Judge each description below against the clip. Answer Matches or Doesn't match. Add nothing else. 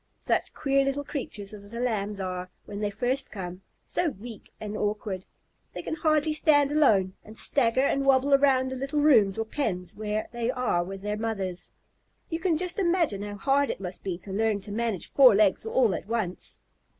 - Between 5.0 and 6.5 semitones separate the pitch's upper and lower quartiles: Matches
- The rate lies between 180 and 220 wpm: Matches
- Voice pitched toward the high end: Matches